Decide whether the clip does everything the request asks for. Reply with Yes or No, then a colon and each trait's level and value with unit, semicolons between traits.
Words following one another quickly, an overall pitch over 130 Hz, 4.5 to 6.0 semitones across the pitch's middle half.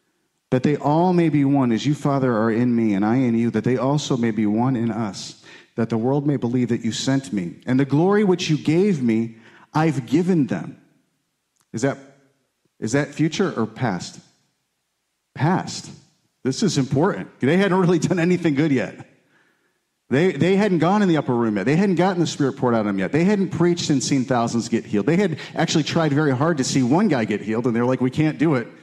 Yes: fast, 225 wpm; medium, 140 Hz; wide, 5.4 semitones